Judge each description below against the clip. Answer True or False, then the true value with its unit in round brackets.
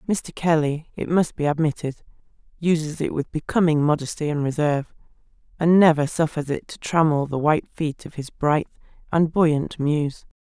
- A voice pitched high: False (155 Hz)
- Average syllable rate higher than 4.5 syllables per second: True (4.9 syllables/s)